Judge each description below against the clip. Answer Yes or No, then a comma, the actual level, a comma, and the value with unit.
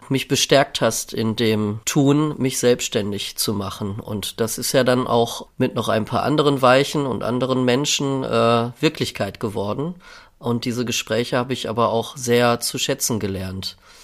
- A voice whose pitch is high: No, low, 120 Hz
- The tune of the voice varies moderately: Yes, average, 3.3 semitones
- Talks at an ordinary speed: Yes, average, 165 wpm